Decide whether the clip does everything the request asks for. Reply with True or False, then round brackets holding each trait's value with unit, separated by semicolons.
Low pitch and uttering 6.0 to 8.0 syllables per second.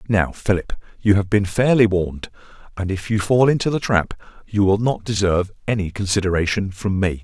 False (100 Hz; 5.5 syllables/s)